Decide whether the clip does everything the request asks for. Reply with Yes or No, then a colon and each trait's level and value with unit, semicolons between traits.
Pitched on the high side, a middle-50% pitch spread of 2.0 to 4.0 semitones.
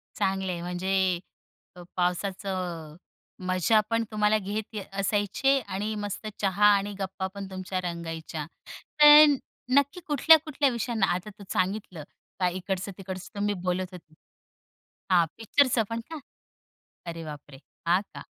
Yes: high, 195 Hz; average, 3.3 semitones